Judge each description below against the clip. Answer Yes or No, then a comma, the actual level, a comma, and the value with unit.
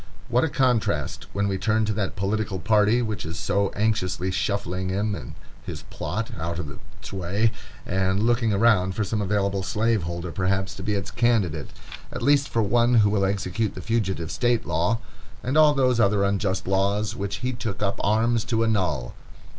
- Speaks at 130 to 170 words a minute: No, average, 180 wpm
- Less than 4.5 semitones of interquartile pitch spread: Yes, average, 3.1 semitones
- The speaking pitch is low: Yes, low, 100 Hz